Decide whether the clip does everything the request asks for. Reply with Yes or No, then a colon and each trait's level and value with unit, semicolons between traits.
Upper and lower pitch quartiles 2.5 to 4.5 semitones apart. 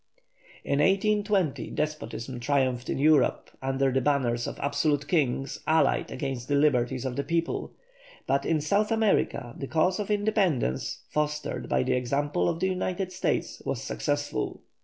No: average, 5.0 semitones